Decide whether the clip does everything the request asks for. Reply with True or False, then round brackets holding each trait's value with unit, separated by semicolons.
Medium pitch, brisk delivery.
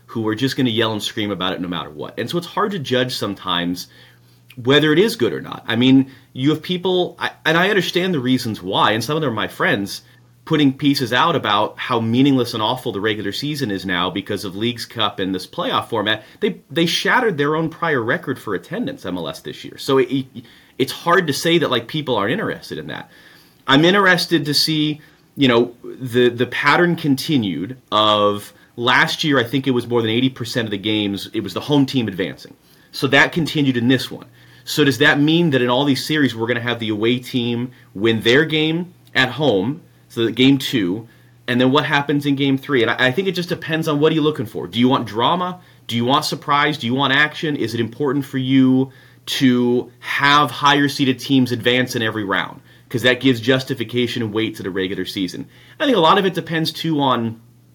False (130 Hz; 220 wpm)